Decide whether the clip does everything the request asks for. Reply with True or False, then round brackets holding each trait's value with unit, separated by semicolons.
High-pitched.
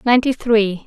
True (230 Hz)